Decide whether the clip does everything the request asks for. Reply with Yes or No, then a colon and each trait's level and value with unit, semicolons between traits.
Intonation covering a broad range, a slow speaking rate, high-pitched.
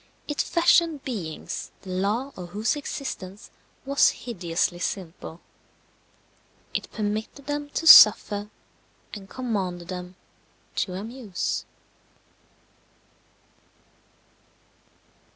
Yes: wide, 6.4 semitones; slow, 80 wpm; high, 210 Hz